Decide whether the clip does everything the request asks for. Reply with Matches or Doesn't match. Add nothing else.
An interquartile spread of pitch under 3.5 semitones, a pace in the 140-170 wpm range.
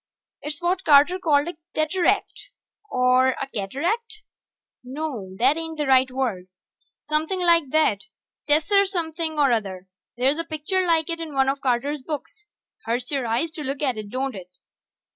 Doesn't match